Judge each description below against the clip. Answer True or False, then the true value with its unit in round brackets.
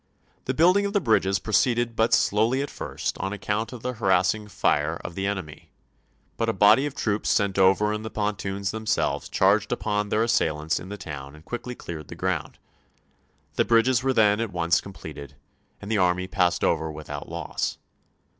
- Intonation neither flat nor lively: True (4.1 semitones)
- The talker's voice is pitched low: True (105 Hz)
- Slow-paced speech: False (185 wpm)